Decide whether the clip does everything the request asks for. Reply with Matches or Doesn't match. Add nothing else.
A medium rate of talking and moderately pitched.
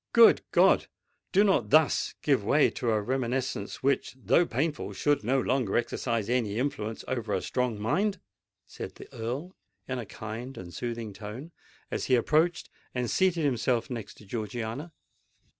Doesn't match